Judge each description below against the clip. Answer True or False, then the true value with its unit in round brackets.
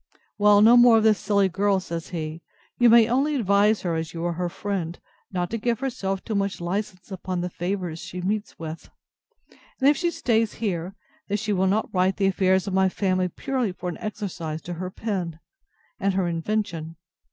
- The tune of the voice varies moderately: True (3.4 semitones)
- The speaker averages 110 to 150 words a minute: False (195 wpm)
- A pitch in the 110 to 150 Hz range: False (190 Hz)